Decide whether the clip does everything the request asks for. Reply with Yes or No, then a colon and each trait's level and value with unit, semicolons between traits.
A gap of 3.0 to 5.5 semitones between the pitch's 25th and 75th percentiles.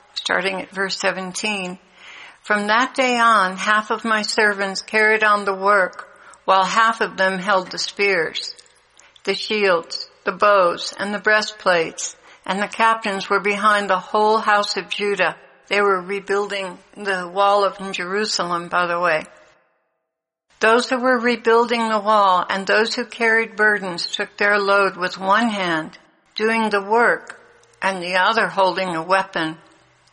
No: narrow, 2.4 semitones